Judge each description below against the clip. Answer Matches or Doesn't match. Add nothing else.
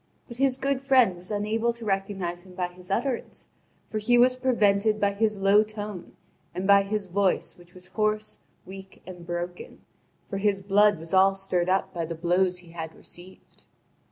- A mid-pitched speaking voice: Doesn't match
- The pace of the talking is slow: Doesn't match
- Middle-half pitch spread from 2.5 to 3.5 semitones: Matches